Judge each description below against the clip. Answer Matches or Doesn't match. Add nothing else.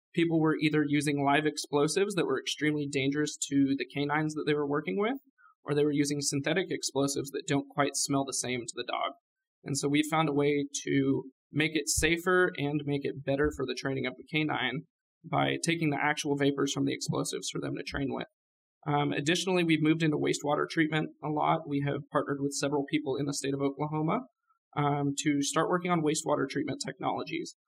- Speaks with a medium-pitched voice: Matches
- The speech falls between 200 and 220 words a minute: Matches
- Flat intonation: Matches